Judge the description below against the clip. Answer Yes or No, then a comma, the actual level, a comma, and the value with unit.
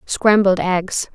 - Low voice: No, high, 190 Hz